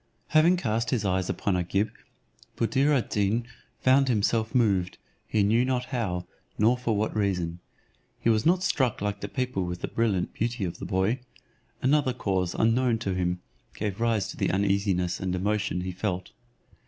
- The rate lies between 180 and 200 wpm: No, average, 170 wpm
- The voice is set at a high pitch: No, low, 105 Hz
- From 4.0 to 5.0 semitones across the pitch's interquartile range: Yes, average, 4.3 semitones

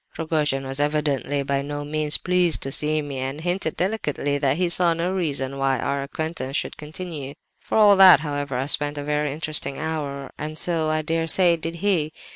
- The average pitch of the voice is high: No, medium, 150 Hz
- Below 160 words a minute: No, average, 195 wpm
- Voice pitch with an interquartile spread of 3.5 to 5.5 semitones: No, average, 2.8 semitones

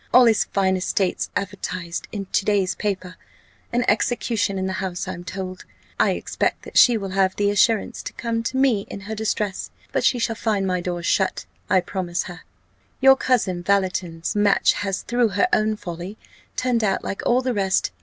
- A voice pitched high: Yes, high, 200 Hz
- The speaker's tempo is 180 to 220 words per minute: Yes, average, 185 wpm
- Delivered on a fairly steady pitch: No, average, 3.0 semitones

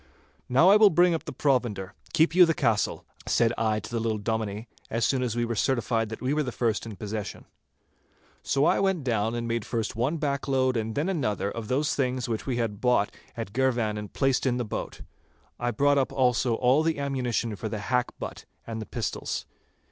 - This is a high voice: No, low, 120 Hz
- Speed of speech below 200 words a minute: No, fast, 205 wpm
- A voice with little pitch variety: No, average, 3.5 semitones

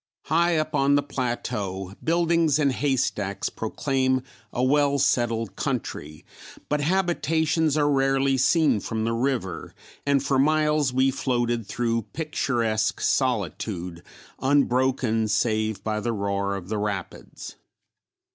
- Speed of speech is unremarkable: No, slow, 120 wpm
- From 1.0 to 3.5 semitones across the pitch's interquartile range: No, average, 4.8 semitones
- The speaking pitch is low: Yes, low, 130 Hz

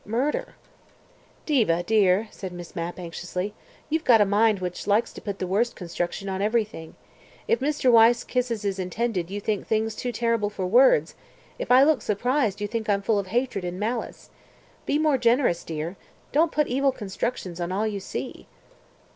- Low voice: No, high, 210 Hz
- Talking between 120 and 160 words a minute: No, average, 180 wpm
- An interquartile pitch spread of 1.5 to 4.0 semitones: No, average, 4.4 semitones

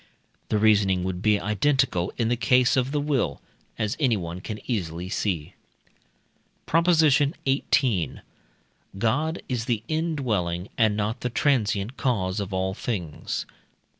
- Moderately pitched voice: No, low, 110 Hz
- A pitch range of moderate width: No, wide, 6.0 semitones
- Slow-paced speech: Yes, slow, 130 wpm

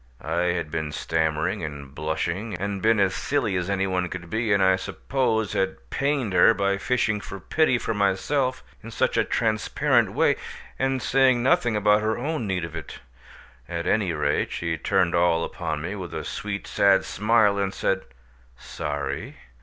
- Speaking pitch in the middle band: No, low, 100 Hz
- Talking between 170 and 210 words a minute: Yes, average, 175 wpm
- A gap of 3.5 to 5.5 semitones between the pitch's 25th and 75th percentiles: Yes, average, 4.5 semitones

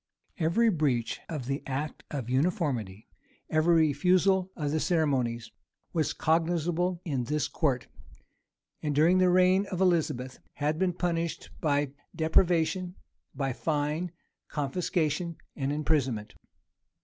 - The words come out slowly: Yes, slow, 115 wpm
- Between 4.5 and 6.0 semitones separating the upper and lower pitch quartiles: No, average, 3.8 semitones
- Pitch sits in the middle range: Yes, medium, 155 Hz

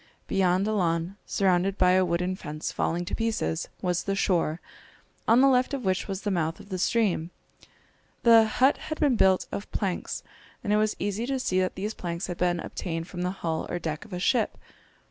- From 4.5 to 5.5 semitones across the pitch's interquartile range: No, average, 3.6 semitones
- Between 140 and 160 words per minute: No, fast, 205 wpm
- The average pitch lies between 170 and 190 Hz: Yes, medium, 185 Hz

